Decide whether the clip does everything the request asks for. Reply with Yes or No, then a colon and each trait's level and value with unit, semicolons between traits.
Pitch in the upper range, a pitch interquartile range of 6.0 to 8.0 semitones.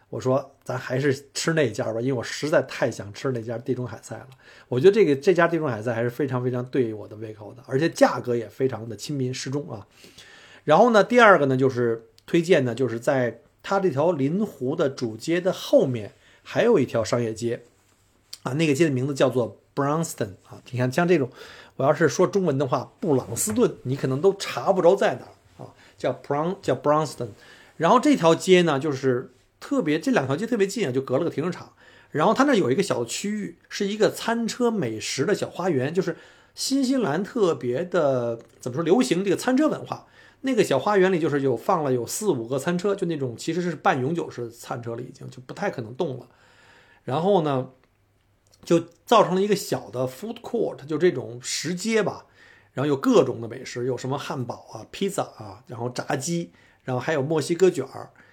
No: low, 135 Hz; wide, 6.3 semitones